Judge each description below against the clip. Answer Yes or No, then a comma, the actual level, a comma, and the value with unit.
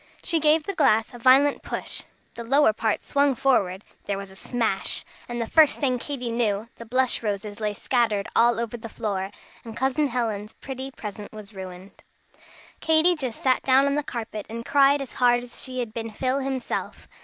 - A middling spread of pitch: Yes, average, 3.9 semitones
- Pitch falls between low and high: No, high, 240 Hz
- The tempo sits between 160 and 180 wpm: No, average, 195 wpm